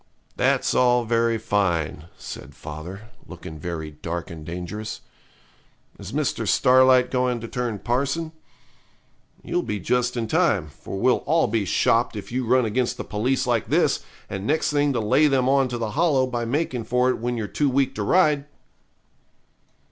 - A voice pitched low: Yes, low, 120 Hz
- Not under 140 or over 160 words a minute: No, average, 170 wpm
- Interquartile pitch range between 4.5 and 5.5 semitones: No, average, 3.9 semitones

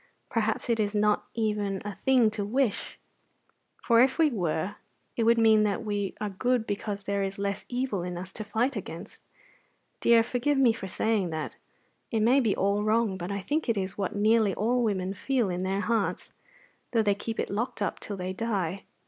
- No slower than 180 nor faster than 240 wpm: Yes, average, 200 wpm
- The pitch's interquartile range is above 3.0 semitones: No, average, 2.7 semitones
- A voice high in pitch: Yes, high, 210 Hz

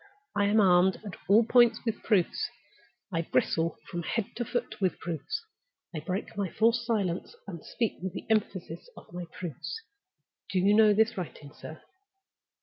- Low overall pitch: No, high, 195 Hz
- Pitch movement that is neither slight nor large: Yes, average, 4.3 semitones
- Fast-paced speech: No, average, 165 wpm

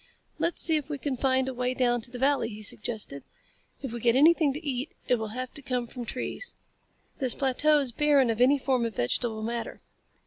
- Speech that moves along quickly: Yes, fast, 215 wpm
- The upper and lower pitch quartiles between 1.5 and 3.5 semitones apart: Yes, average, 2.9 semitones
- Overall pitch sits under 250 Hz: No, very high, 255 Hz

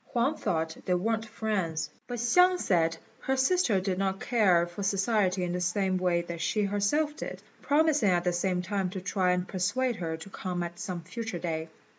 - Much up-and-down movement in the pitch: No, average, 4.1 semitones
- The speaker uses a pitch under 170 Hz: No, high, 190 Hz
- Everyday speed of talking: Yes, average, 195 wpm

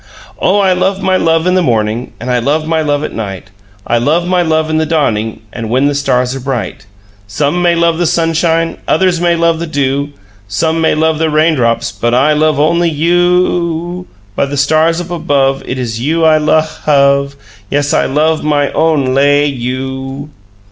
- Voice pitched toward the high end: No, medium, 150 Hz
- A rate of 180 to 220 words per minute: Yes, average, 195 wpm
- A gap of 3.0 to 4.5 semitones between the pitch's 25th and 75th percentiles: Yes, average, 3.6 semitones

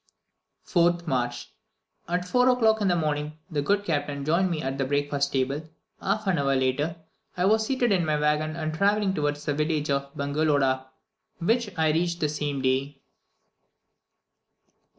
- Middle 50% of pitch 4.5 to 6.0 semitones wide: No, average, 3.9 semitones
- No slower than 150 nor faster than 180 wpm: Yes, average, 160 wpm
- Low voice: No, medium, 155 Hz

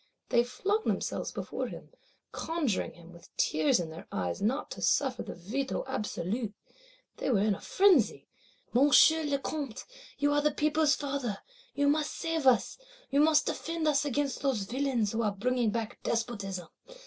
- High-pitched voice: Yes, very high, 260 Hz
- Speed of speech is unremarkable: Yes, average, 165 wpm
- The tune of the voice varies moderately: No, wide, 5.7 semitones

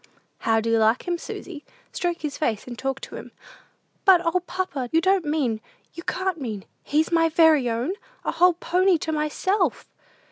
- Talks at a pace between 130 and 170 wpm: No, average, 185 wpm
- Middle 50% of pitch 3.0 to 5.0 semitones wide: No, wide, 5.6 semitones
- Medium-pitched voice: No, very high, 320 Hz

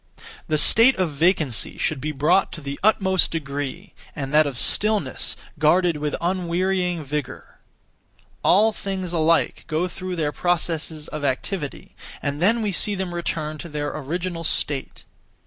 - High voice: No, medium, 165 Hz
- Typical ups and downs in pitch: Yes, average, 3.8 semitones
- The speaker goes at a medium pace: Yes, average, 145 wpm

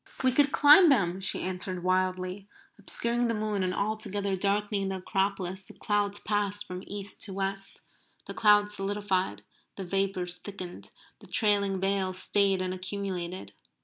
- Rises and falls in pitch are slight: Yes, narrow, 1.9 semitones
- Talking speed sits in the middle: Yes, average, 145 wpm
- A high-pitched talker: Yes, high, 195 Hz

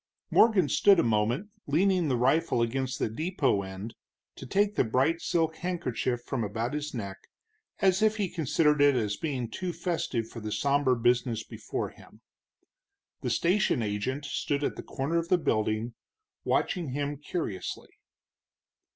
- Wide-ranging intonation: Yes, wide, 6.3 semitones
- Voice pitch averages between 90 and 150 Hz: Yes, medium, 140 Hz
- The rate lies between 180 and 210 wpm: No, average, 155 wpm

